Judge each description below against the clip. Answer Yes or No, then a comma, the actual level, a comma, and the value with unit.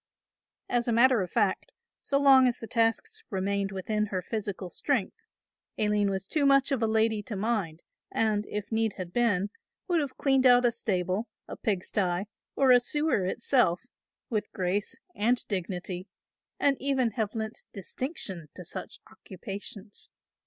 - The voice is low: No, high, 220 Hz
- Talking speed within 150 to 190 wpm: Yes, average, 155 wpm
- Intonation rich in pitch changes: No, average, 4.3 semitones